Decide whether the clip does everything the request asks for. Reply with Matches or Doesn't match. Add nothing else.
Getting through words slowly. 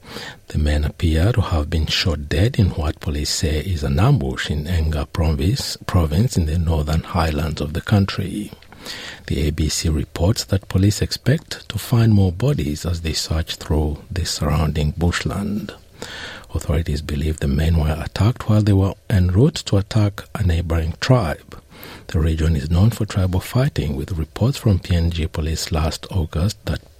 Doesn't match